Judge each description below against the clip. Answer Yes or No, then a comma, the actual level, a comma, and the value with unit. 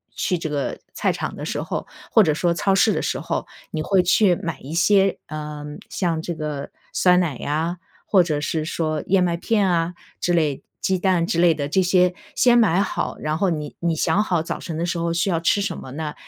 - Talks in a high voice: No, medium, 170 Hz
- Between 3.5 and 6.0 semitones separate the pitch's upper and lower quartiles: No, average, 2.8 semitones